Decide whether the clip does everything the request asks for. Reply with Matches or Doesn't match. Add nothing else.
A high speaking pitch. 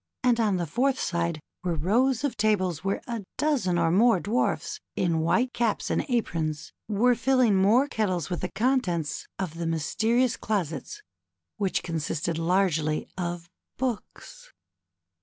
Matches